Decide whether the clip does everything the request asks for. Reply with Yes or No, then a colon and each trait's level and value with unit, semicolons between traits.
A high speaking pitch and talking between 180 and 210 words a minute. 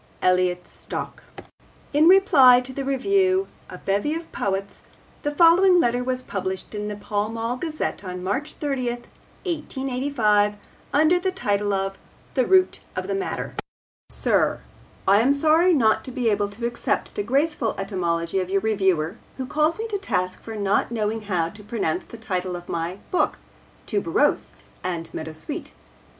No: high, 225 Hz; average, 160 wpm